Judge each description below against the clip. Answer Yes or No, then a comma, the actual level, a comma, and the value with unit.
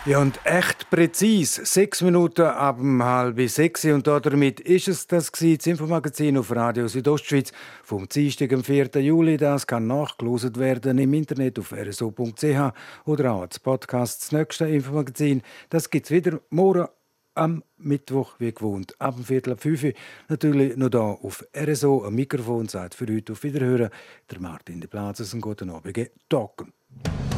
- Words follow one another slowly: No, average, 165 wpm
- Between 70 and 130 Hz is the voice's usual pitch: No, medium, 140 Hz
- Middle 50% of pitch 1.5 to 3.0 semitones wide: No, average, 3.9 semitones